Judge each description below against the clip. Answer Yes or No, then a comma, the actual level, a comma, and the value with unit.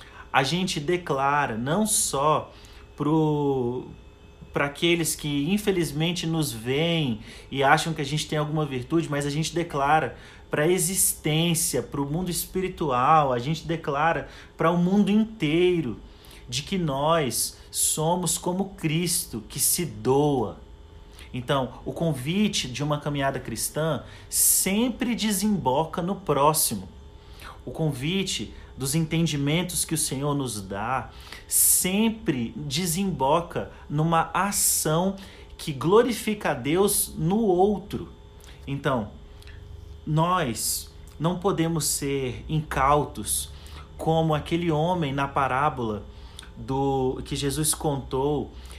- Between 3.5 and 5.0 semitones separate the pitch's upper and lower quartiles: No, wide, 5.5 semitones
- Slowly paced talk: Yes, slow, 115 wpm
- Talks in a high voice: No, medium, 150 Hz